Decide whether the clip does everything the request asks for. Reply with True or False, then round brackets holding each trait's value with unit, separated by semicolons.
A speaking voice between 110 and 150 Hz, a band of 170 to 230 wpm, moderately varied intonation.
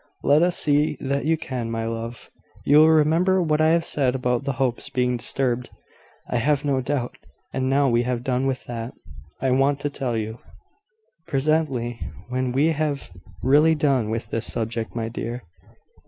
True (135 Hz; 180 wpm; 3.7 semitones)